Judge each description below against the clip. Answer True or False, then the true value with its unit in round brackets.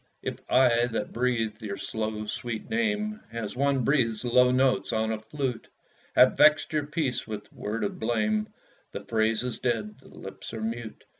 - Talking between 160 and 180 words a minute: True (170 wpm)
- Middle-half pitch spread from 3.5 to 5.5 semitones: False (2.9 semitones)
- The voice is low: True (115 Hz)